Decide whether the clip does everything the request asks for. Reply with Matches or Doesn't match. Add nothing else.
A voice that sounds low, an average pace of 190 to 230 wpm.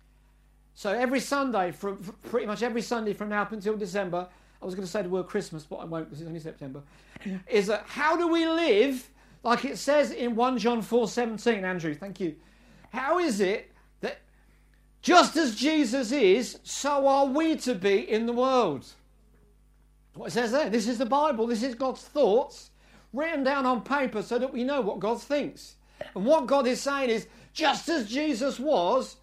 Doesn't match